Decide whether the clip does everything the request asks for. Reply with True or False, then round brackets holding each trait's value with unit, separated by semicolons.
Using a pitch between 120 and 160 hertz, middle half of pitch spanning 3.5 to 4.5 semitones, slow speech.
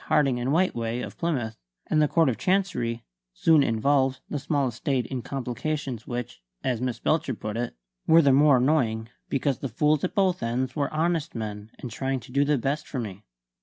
False (135 Hz; 4.1 semitones; 195 wpm)